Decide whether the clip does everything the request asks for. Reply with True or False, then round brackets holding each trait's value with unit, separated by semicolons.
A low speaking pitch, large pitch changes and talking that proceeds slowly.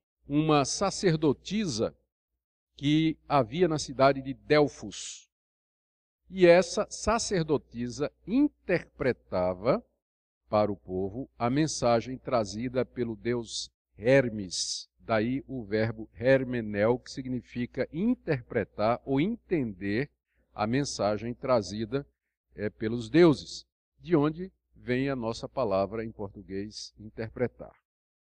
True (120 Hz; 5.9 semitones; 95 wpm)